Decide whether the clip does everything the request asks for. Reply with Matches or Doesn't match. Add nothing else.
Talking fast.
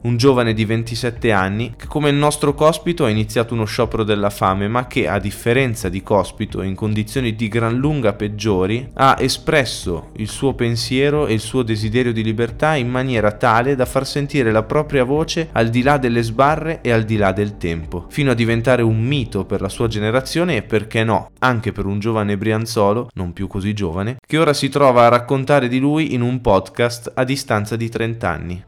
Matches